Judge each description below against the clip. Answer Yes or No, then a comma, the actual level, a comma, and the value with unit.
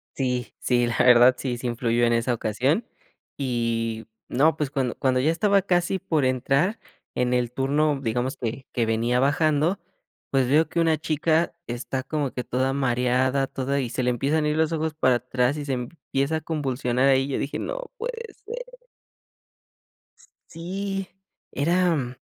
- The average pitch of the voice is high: No, low, 135 Hz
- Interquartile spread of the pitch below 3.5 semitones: No, average, 4.3 semitones